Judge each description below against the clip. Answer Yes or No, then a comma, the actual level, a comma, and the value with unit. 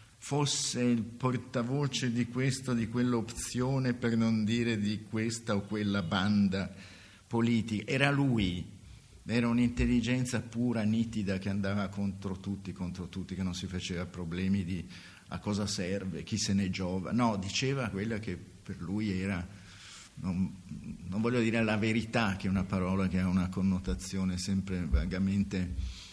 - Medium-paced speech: Yes, average, 145 wpm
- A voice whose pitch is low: Yes, low, 100 Hz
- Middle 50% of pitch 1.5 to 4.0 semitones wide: Yes, average, 3.7 semitones